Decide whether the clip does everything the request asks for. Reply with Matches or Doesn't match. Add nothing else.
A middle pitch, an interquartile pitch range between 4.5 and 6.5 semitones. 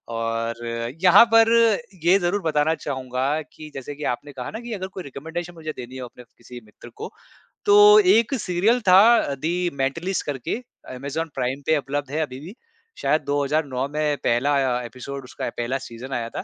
Matches